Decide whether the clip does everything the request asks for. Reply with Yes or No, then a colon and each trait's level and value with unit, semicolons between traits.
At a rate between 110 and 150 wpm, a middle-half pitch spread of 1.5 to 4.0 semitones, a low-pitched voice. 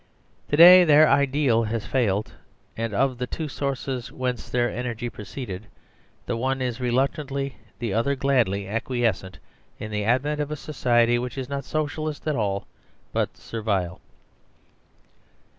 Yes: average, 145 wpm; average, 3.7 semitones; low, 125 Hz